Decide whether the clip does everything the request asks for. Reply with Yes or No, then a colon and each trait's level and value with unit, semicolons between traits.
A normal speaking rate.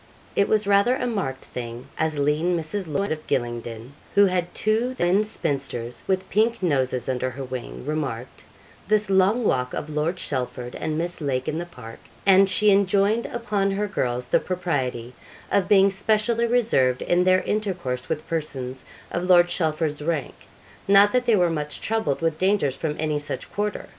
Yes: average, 175 wpm